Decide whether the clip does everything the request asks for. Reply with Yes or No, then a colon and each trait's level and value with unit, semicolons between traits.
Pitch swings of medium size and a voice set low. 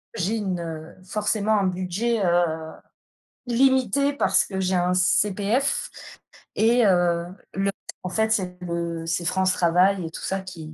No: average, 3.6 semitones; medium, 185 Hz